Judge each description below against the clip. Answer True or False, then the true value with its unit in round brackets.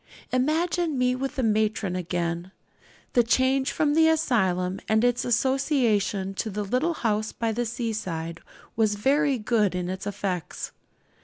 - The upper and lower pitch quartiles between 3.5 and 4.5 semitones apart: False (5.3 semitones)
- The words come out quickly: False (145 wpm)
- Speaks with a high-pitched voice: True (225 Hz)